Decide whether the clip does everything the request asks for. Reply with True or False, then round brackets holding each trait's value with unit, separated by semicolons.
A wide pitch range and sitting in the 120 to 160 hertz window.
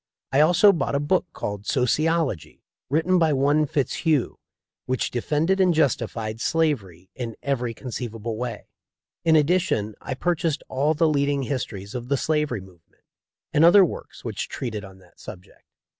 True (5.7 semitones; 140 Hz)